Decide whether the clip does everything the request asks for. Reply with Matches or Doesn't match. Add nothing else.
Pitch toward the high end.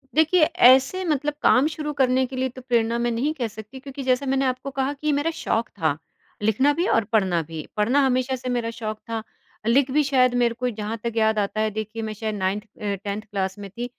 Matches